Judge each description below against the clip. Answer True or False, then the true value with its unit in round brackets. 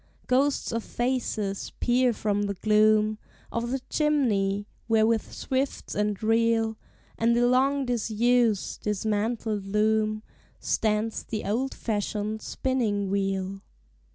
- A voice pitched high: True (220 Hz)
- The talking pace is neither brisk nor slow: False (115 wpm)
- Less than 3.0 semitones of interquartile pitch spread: True (2.6 semitones)